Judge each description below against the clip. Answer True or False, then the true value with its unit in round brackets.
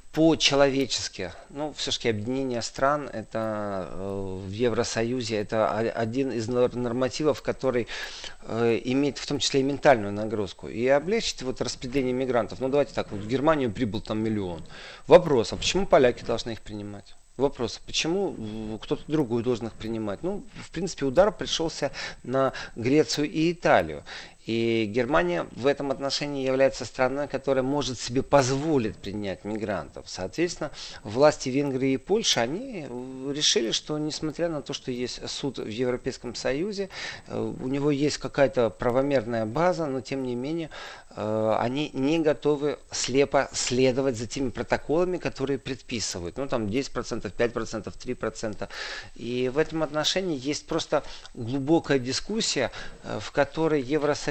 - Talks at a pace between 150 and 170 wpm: False (140 wpm)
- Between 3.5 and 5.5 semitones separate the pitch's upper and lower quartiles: True (4.1 semitones)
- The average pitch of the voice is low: True (130 Hz)